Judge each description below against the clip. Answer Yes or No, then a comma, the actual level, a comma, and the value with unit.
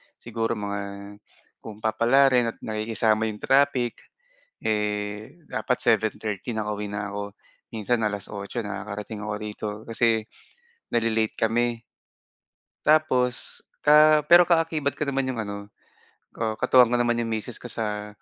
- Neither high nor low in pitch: No, low, 110 Hz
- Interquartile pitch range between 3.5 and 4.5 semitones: No, average, 2.7 semitones